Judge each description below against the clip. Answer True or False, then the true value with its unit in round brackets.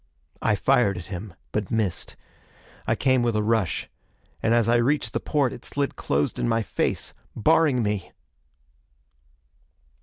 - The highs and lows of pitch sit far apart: False (3.5 semitones)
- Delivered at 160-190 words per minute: False (150 wpm)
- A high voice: False (115 Hz)